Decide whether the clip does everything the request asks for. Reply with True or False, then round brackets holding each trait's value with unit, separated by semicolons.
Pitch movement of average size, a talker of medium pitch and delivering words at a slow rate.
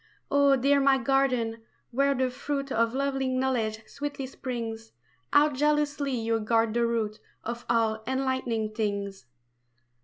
False (3.4 semitones; 250 Hz; 130 wpm)